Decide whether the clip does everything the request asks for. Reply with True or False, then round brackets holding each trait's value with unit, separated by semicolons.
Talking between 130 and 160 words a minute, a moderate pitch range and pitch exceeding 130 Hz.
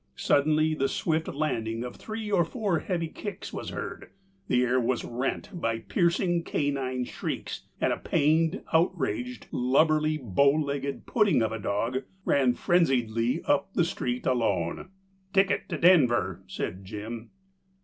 False (140 wpm; 5.9 semitones; 140 Hz)